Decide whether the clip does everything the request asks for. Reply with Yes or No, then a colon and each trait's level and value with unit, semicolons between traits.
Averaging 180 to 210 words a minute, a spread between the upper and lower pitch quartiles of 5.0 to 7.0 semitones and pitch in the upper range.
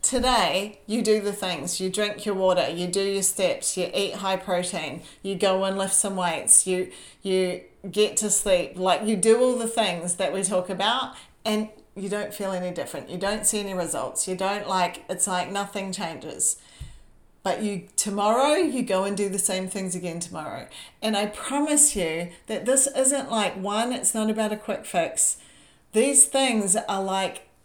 No: average, 190 wpm; narrow, 2.6 semitones; high, 195 Hz